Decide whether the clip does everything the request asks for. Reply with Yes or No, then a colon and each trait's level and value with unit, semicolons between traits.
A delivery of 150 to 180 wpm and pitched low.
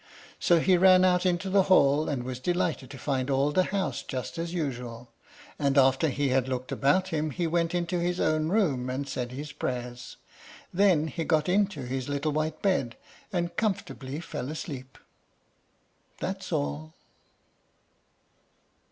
No: average, 155 wpm; medium, 150 Hz